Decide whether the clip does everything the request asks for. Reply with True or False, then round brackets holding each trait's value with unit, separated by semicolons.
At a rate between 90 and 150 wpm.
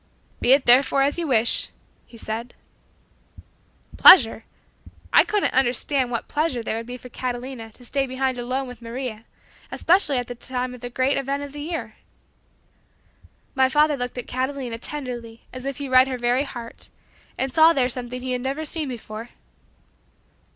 False (170 wpm)